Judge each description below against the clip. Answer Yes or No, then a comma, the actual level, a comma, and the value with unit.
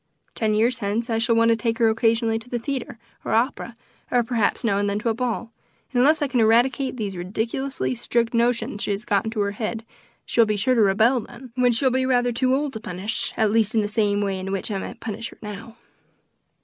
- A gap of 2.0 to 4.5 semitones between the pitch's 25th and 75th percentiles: Yes, narrow, 2.5 semitones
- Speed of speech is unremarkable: No, fast, 240 wpm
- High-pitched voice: Yes, high, 230 Hz